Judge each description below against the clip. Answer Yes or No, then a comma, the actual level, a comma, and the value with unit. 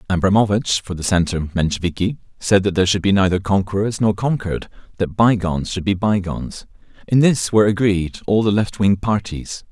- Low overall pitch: Yes, low, 100 Hz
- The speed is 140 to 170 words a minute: Yes, average, 165 wpm